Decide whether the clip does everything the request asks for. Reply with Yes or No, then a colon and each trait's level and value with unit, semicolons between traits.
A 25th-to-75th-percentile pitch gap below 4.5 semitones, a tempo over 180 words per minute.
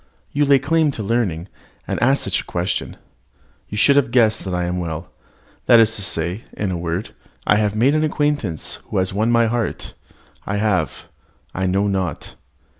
No: average, 4.8 semitones; average, 190 wpm